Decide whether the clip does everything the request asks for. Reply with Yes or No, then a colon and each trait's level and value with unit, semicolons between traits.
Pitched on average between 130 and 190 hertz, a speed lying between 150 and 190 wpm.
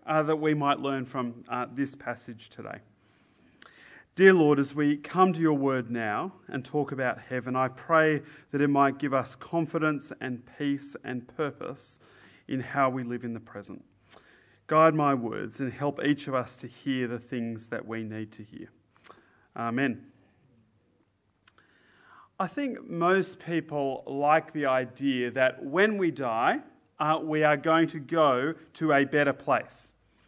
Yes: medium, 140 Hz; average, 160 wpm